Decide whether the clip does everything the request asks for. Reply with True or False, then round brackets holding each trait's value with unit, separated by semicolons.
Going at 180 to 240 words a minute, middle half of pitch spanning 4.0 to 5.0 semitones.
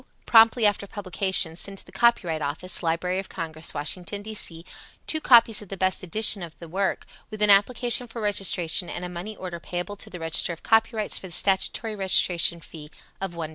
False (200 wpm; 3.6 semitones)